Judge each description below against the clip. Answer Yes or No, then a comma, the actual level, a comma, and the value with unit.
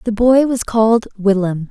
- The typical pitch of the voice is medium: No, high, 220 Hz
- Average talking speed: Yes, average, 175 wpm